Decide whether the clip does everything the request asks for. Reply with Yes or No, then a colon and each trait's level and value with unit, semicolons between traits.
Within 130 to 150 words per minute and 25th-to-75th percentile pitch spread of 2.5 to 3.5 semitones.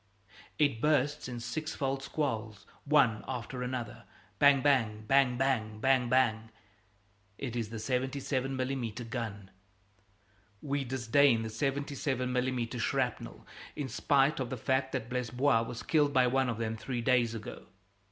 Yes: average, 140 wpm; average, 2.9 semitones